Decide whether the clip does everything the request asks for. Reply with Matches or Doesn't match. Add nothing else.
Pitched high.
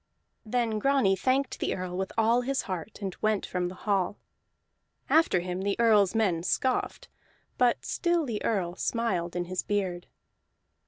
Matches